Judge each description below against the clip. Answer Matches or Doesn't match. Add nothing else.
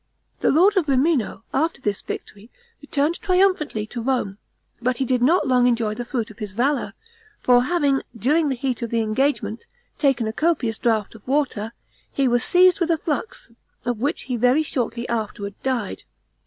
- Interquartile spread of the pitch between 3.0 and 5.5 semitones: Matches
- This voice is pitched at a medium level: Doesn't match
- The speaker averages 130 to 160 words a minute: Doesn't match